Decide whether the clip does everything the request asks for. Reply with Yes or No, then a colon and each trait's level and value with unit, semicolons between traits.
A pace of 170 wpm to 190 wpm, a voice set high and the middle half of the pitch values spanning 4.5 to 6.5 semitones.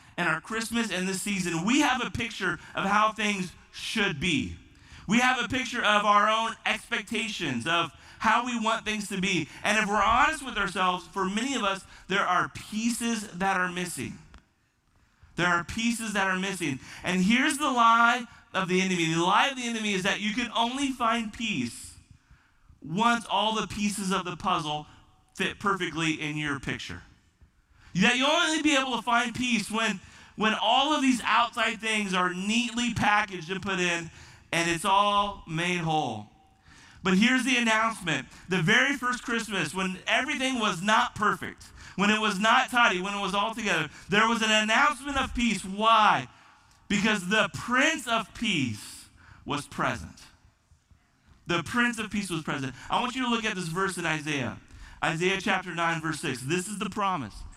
Yes: average, 180 wpm; high, 200 Hz; average, 5.3 semitones